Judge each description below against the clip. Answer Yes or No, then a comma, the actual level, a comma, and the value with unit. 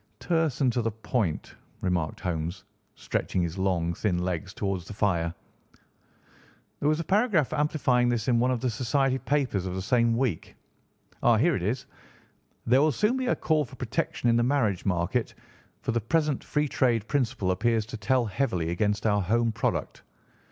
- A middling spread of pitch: No, wide, 5.9 semitones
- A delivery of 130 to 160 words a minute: No, average, 180 wpm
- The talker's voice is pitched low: Yes, low, 115 Hz